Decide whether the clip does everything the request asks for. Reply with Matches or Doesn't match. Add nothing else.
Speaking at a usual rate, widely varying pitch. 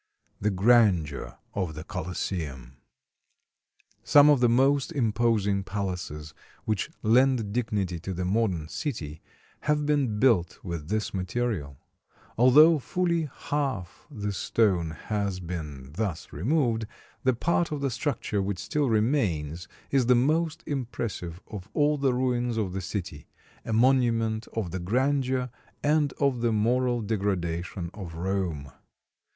Doesn't match